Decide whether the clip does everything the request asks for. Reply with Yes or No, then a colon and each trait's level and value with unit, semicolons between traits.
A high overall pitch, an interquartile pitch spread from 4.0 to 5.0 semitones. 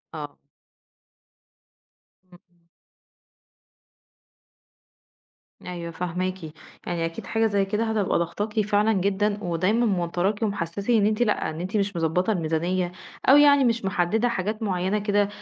No: high, 195 Hz; average, 3.3 semitones